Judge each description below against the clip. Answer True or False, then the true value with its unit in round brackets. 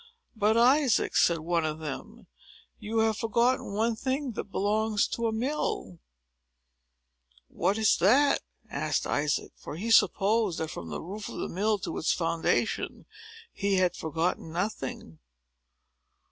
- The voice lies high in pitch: True (205 Hz)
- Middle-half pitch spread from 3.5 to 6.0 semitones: True (5.4 semitones)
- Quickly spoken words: False (140 wpm)